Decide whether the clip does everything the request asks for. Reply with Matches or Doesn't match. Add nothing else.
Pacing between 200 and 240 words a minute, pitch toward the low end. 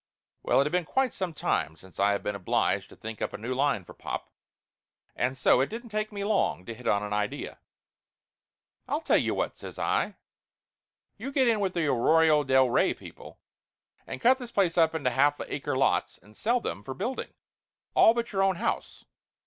Doesn't match